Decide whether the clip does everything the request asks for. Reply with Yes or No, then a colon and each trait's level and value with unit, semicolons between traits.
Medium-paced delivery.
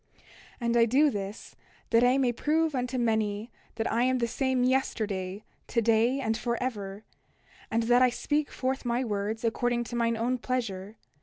Yes: average, 170 wpm